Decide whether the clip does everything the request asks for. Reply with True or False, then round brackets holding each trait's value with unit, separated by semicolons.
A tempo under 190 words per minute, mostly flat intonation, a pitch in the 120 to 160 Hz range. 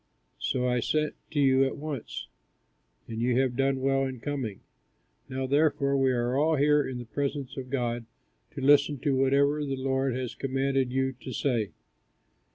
True (170 wpm; 1.8 semitones; 135 Hz)